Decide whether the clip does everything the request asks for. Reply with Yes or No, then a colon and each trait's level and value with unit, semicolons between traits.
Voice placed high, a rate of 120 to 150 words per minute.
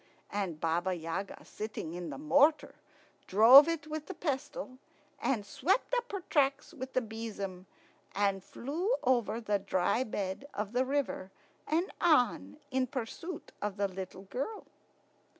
Yes: high, 240 Hz; average, 145 wpm